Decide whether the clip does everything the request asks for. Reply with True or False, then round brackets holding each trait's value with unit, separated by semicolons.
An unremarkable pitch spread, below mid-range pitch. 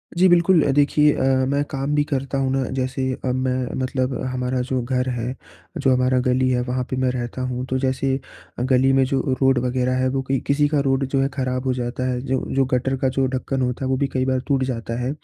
False (1.1 semitones; 130 Hz)